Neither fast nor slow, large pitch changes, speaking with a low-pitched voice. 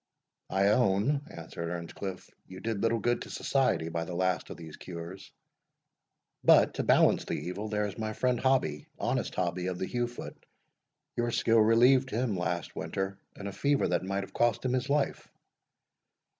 No: average, 175 wpm; average, 4.9 semitones; low, 100 Hz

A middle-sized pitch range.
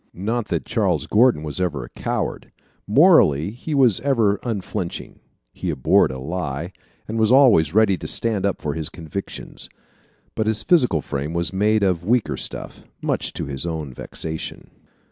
No: wide, 5.8 semitones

